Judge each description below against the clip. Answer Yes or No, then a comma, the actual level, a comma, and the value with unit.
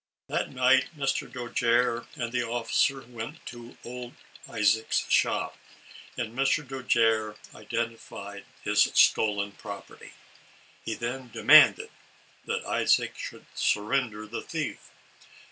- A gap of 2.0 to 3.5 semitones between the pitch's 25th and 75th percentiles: Yes, narrow, 2.6 semitones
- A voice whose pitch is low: Yes, low, 120 Hz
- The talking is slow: Yes, slow, 110 wpm